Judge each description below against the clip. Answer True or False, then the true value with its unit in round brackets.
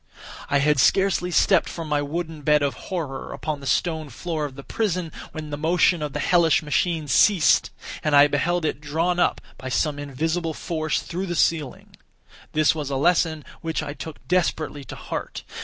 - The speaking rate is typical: True (185 wpm)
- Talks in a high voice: False (155 Hz)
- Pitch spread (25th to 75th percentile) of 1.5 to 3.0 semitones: True (2.7 semitones)